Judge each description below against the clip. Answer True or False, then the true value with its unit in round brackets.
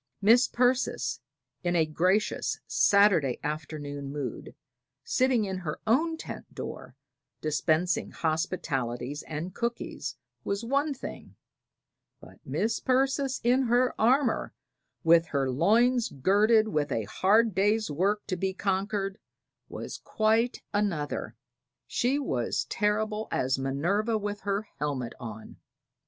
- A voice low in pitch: False (195 Hz)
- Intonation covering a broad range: True (6.9 semitones)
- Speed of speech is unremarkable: False (115 wpm)